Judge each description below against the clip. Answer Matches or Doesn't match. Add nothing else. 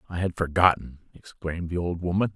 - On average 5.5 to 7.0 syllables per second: Matches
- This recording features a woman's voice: Doesn't match